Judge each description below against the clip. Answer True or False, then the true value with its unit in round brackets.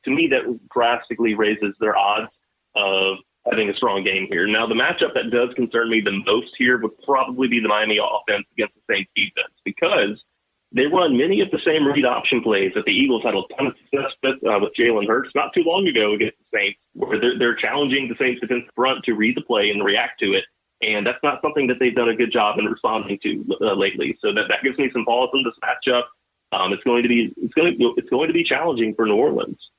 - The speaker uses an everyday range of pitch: True (3.4 semitones)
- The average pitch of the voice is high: False (120 Hz)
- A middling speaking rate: False (240 wpm)